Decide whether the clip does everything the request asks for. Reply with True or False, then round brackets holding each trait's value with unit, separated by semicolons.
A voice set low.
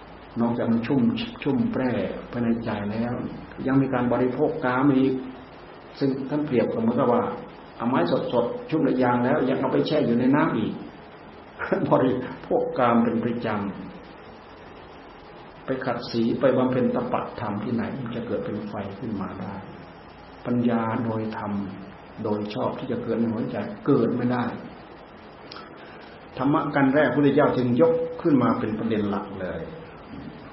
True (120 Hz)